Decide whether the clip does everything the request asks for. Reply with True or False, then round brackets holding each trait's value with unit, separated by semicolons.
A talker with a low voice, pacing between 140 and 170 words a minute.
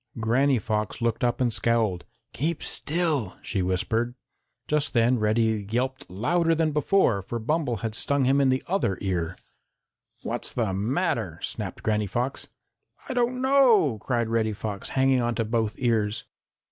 True (120 Hz; 155 wpm)